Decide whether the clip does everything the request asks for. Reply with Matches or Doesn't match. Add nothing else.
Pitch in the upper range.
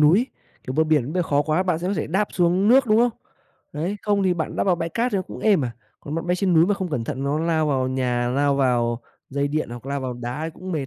Doesn't match